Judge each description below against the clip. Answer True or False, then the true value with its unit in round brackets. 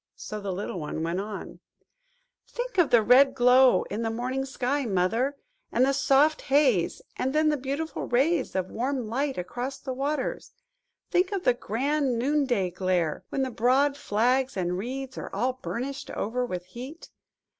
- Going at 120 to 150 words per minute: False (165 wpm)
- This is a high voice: True (255 Hz)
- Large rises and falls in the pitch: False (4.3 semitones)